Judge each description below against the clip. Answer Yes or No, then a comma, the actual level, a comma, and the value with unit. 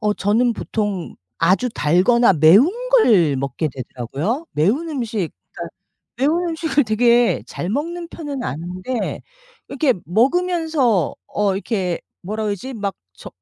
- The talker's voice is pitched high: Yes, high, 220 Hz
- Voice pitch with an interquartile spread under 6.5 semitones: No, wide, 7.1 semitones